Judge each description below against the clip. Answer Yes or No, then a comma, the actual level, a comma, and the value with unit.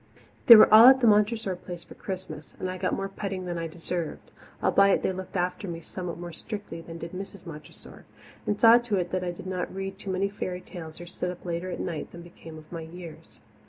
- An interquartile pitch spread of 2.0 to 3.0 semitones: Yes, narrow, 2.4 semitones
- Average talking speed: No, fast, 225 wpm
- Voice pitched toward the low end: No, medium, 180 Hz